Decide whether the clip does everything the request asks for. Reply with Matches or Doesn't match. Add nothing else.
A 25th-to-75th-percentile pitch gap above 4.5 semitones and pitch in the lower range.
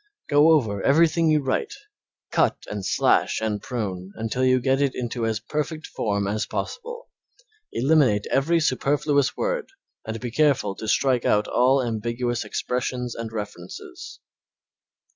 Matches